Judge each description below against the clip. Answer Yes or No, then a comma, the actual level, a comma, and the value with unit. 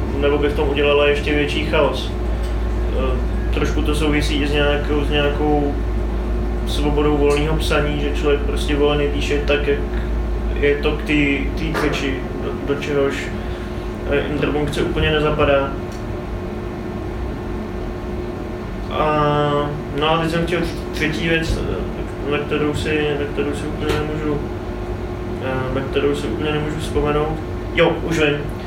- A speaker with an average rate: Yes, average, 130 wpm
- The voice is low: No, medium, 145 Hz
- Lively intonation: Yes, wide, 8.3 semitones